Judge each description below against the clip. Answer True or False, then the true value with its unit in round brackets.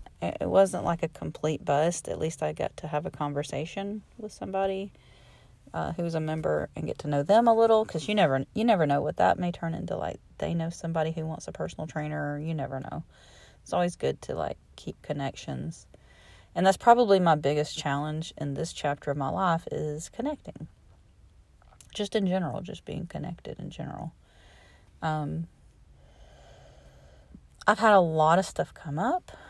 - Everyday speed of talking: True (180 wpm)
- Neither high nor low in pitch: True (160 Hz)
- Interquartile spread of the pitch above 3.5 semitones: True (4.5 semitones)